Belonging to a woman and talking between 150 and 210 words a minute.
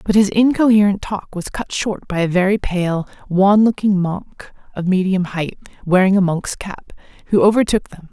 Yes: female; average, 175 wpm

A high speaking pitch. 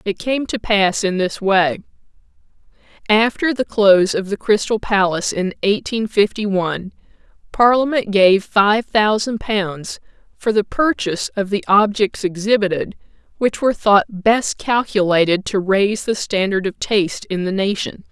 Yes: high, 205 Hz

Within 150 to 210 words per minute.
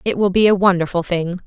No: fast, 245 wpm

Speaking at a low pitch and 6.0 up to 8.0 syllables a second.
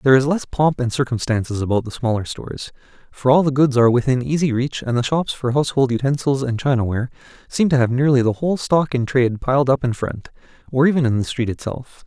Yes: low, 130 Hz; 6.3 syllables/s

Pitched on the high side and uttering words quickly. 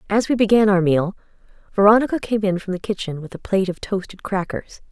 Yes: high, 200 Hz; fast, 210 wpm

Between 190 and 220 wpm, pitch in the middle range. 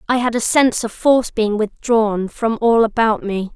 No: average, 200 wpm; high, 225 Hz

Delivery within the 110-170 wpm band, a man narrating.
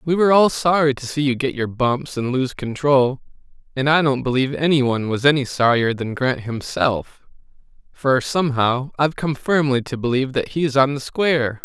No: average, 190 wpm; male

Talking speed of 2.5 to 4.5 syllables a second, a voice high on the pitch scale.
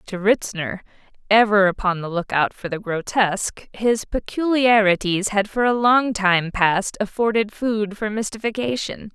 Yes: 4.4 syllables/s; high, 205 Hz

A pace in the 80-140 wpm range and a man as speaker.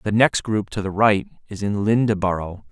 No: average, 200 wpm; male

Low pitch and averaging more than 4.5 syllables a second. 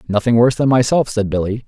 Yes: low, 115 Hz; 6.6 syllables/s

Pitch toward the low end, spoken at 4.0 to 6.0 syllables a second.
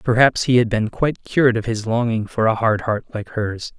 Yes: low, 115 Hz; 5.4 syllables/s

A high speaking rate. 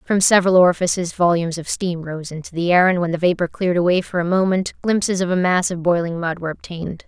Yes: fast, 235 wpm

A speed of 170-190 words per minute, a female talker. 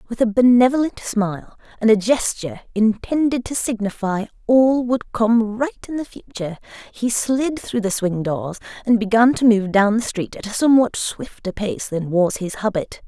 Yes: average, 180 wpm; female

